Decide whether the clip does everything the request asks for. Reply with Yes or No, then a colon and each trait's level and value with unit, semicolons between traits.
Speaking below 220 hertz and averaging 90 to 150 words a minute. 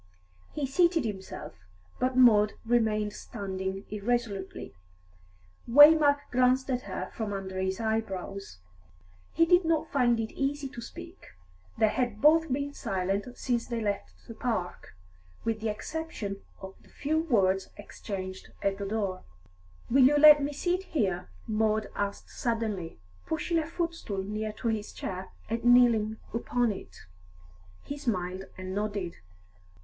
No: high, 225 Hz; average, 140 wpm